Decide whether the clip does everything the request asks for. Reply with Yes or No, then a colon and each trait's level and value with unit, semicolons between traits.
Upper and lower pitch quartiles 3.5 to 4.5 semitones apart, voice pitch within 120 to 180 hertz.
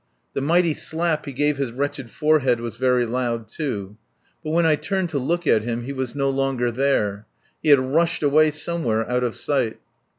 Yes: average, 4.2 semitones; low, 135 Hz